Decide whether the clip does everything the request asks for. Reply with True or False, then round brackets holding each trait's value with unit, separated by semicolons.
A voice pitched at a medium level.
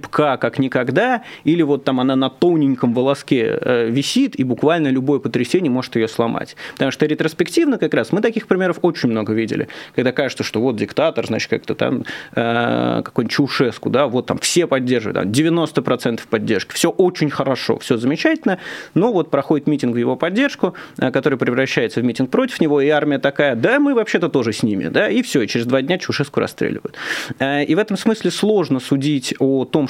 True (145 Hz)